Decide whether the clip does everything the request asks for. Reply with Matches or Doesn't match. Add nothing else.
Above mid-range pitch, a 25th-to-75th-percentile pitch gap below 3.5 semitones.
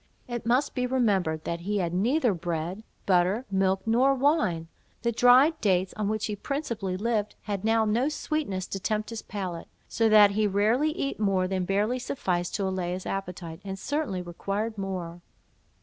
Doesn't match